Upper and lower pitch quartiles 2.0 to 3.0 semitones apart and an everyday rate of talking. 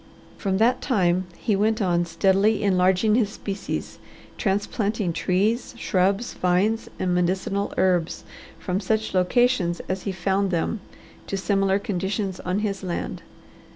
No: narrow, 2.5 semitones; slow, 130 wpm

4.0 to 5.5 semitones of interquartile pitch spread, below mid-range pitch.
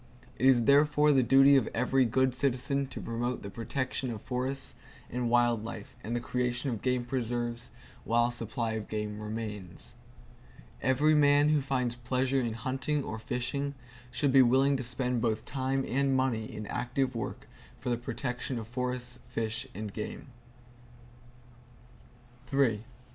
No: narrow, 2.4 semitones; low, 125 Hz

